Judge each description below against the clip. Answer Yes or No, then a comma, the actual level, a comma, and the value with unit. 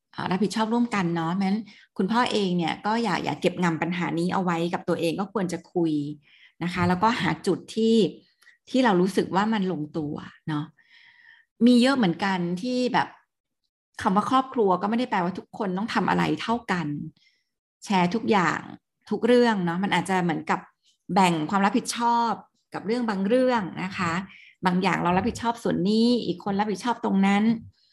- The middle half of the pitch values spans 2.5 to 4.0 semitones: No, average, 4.6 semitones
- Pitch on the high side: Yes, high, 195 Hz